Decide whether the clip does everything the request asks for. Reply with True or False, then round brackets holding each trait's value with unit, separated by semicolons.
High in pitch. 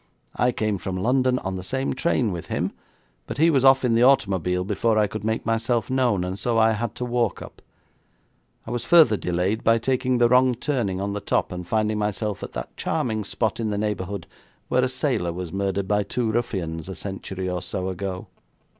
False (110 Hz)